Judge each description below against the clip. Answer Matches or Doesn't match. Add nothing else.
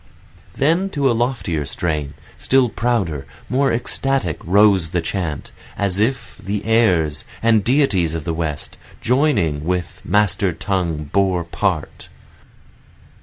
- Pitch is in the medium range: Doesn't match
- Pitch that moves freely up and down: Matches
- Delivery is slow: Matches